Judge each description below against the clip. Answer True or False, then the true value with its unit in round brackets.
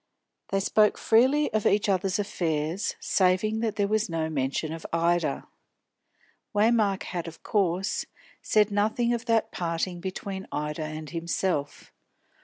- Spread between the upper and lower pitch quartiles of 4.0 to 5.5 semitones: True (4.3 semitones)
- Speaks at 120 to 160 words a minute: True (135 wpm)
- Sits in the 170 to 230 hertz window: True (190 Hz)